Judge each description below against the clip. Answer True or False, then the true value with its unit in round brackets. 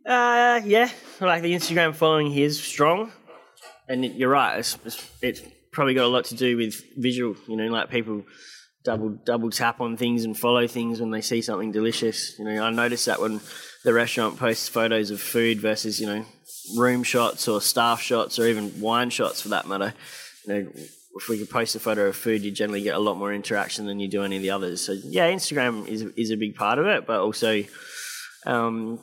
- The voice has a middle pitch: False (115 Hz)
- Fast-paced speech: True (215 wpm)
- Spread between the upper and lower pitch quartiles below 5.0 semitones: True (2.7 semitones)